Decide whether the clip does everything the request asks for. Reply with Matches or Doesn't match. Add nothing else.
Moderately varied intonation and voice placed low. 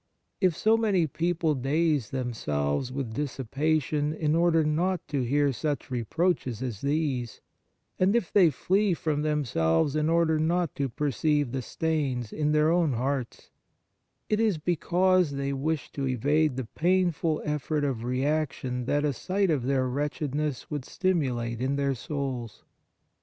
Doesn't match